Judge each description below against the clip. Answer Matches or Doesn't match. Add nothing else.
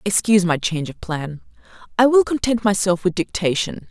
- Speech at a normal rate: Matches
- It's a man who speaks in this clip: Doesn't match